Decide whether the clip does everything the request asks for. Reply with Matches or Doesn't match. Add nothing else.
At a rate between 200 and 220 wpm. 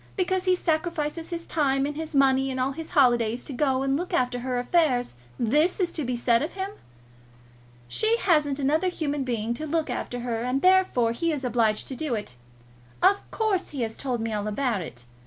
Matches